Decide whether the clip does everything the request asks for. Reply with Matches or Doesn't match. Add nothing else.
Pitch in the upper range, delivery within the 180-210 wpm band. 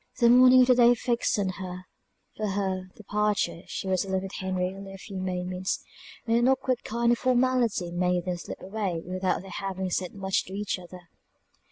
Matches